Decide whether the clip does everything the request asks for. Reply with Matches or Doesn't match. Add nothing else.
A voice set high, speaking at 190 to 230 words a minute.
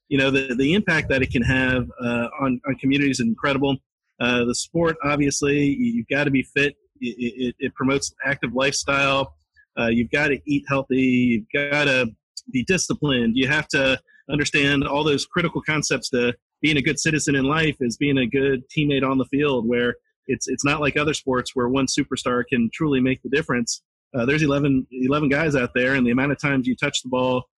Doesn't match